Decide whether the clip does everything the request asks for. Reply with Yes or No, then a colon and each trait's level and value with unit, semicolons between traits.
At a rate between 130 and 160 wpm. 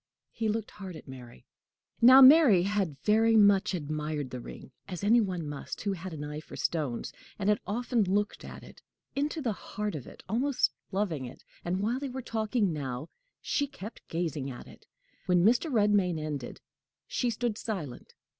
No: average, 180 wpm